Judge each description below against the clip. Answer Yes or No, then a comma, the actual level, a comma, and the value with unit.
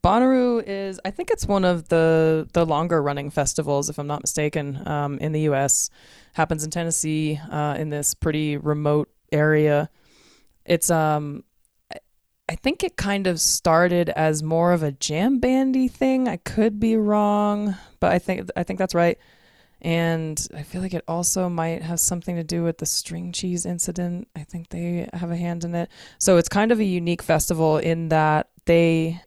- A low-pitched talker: No, medium, 170 Hz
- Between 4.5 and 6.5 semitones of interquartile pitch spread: No, average, 2.9 semitones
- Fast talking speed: No, average, 185 wpm